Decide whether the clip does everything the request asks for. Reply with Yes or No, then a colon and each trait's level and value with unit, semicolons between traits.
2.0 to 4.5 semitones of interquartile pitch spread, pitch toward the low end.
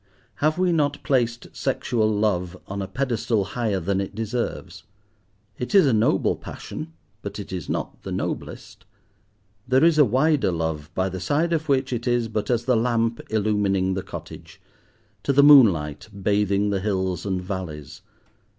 No: average, 5.2 semitones; low, 110 Hz